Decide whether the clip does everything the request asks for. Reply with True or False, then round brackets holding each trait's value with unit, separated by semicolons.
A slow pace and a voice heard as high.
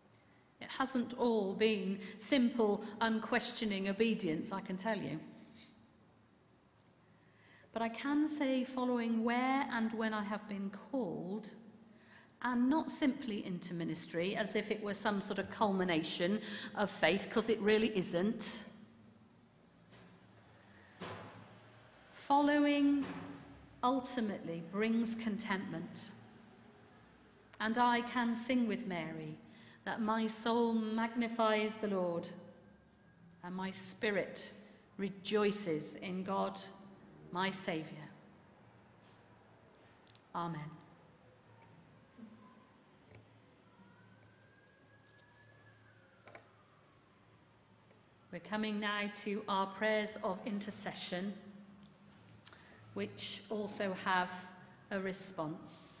True (85 wpm; 205 Hz)